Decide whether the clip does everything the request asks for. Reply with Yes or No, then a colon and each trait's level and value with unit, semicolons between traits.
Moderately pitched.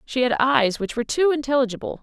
No: high, 245 Hz